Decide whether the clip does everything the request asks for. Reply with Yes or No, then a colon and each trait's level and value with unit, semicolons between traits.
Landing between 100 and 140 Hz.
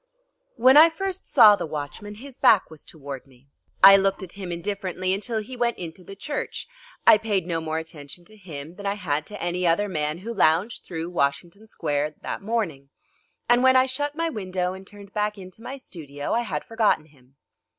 No: high, 190 Hz